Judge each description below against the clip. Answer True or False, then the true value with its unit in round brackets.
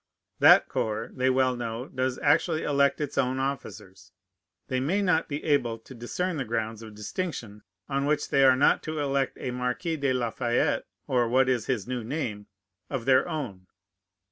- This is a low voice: True (130 Hz)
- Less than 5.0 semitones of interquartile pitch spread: True (3.4 semitones)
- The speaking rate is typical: True (180 wpm)